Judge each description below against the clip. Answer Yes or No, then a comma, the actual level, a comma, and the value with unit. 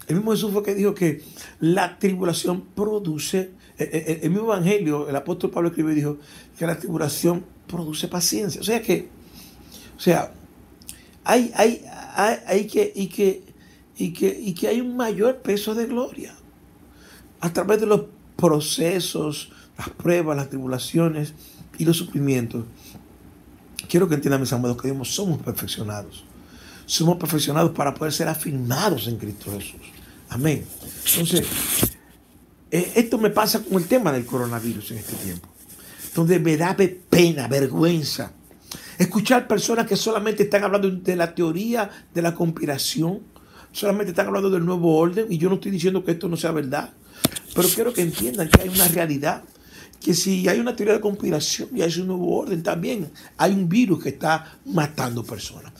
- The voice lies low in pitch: No, medium, 170 Hz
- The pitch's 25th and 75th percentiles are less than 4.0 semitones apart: No, average, 4.9 semitones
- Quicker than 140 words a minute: Yes, average, 150 wpm